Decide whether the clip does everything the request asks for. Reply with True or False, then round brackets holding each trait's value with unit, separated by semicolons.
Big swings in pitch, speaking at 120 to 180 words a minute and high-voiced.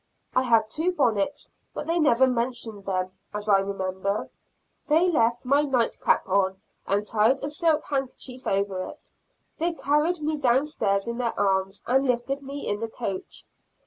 True (6.1 semitones; 170 wpm; 240 Hz)